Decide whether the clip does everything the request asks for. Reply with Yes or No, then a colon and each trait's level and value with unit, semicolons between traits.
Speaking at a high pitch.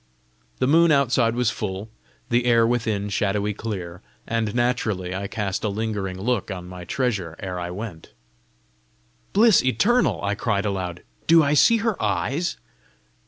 No: low, 110 Hz